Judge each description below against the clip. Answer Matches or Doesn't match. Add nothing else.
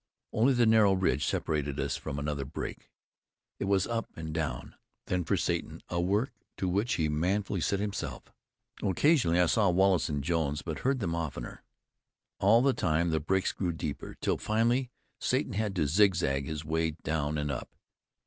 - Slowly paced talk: Doesn't match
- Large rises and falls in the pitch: Doesn't match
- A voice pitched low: Matches